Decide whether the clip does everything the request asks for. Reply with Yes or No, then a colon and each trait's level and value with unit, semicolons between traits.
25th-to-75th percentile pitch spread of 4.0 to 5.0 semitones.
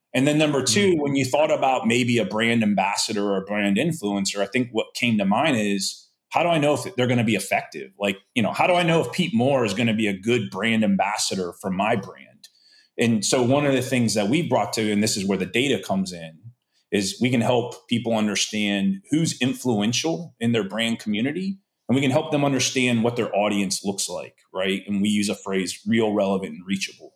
Yes: average, 4.4 semitones